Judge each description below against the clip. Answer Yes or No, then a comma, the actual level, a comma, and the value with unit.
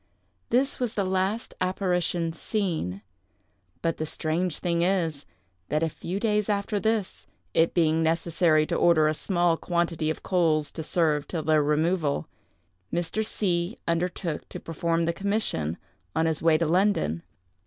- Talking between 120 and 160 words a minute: Yes, average, 155 wpm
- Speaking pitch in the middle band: Yes, medium, 170 Hz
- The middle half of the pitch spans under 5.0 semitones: Yes, average, 3.1 semitones